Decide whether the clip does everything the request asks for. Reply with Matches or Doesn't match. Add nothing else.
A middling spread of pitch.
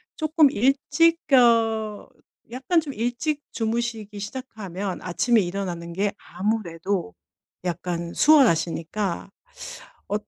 Doesn't match